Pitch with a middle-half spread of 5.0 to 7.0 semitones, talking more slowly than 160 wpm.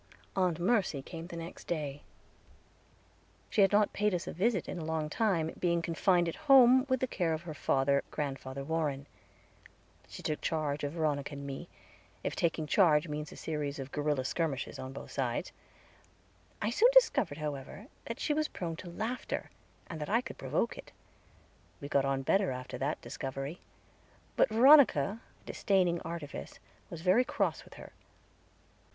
No: wide, 5.4 semitones; average, 165 wpm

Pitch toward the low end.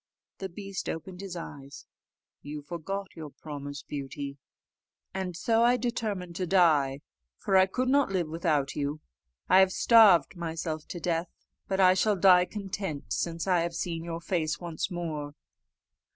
No: medium, 170 Hz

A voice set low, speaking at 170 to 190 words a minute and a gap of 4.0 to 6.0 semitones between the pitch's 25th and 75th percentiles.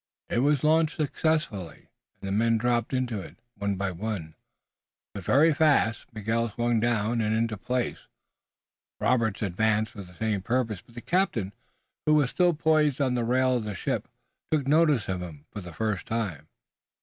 Yes: low, 115 Hz; average, 175 wpm; average, 4.5 semitones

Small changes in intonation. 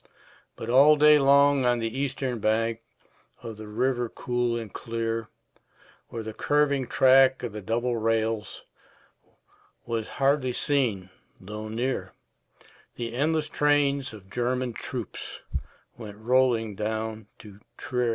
No: average, 3.1 semitones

